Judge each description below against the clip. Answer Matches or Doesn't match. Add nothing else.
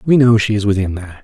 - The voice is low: Matches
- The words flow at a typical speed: Doesn't match